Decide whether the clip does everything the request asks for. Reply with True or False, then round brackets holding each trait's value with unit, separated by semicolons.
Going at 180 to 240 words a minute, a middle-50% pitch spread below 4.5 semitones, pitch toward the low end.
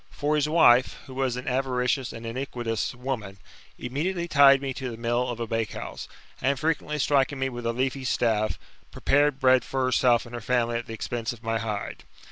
True (195 wpm; 2.5 semitones; 125 Hz)